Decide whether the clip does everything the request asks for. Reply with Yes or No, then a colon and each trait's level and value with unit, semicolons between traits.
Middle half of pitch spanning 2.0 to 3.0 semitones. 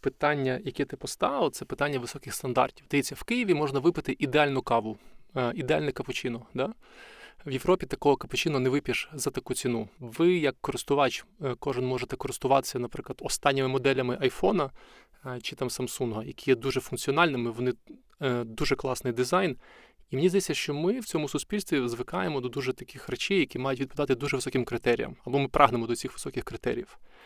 Yes: narrow, 2.6 semitones